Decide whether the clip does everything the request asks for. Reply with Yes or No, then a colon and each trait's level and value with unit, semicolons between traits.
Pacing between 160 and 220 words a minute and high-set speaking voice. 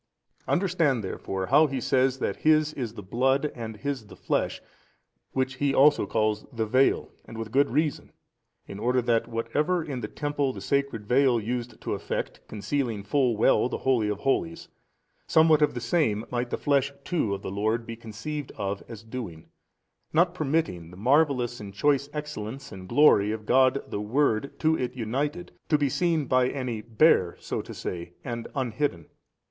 No: average, 175 wpm; low, 125 Hz